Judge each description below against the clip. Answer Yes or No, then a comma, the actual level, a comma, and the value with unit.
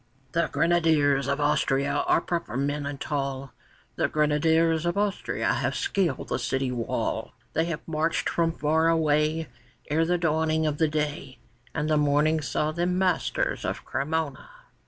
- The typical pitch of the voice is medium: Yes, medium, 155 Hz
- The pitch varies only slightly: Yes, narrow, 2.1 semitones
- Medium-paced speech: Yes, average, 155 wpm